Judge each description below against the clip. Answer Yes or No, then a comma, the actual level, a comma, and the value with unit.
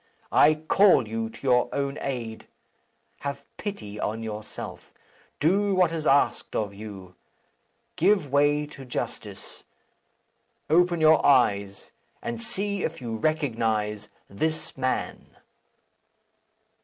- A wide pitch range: Yes, wide, 6.1 semitones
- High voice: No, low, 135 Hz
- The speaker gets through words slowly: Yes, slow, 110 wpm